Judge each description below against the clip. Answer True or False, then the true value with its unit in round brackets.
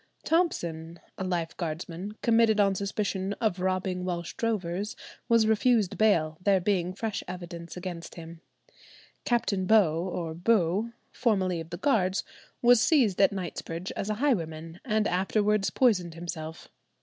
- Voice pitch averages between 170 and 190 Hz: True (185 Hz)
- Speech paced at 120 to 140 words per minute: True (135 wpm)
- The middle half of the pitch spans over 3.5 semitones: True (3.9 semitones)